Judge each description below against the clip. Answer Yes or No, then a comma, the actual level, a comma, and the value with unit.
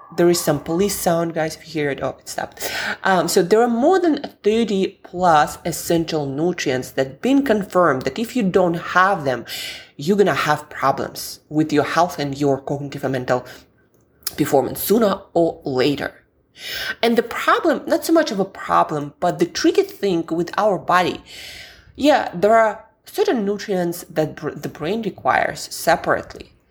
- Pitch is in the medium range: Yes, medium, 175 Hz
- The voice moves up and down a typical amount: No, wide, 6.3 semitones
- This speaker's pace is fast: No, average, 175 wpm